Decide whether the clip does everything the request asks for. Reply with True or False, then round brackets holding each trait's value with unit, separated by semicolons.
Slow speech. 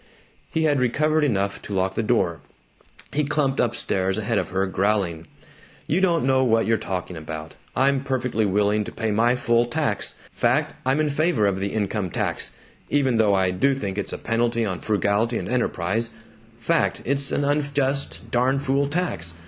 False (180 wpm)